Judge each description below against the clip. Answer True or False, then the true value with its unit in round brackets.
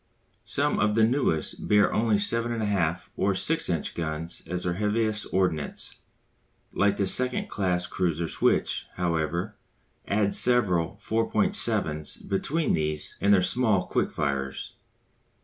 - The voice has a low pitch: True (95 Hz)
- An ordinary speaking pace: False (130 wpm)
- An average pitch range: True (4.4 semitones)